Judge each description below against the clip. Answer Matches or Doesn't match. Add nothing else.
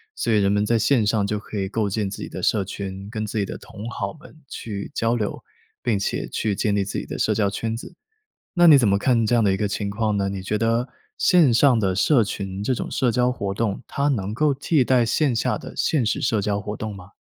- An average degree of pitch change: Matches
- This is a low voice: Matches